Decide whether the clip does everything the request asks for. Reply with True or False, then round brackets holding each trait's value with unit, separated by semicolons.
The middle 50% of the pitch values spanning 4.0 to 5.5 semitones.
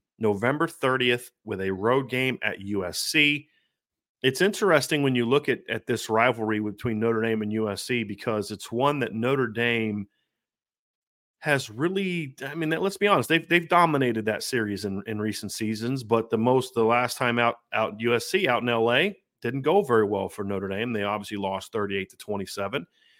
True (4.8 semitones)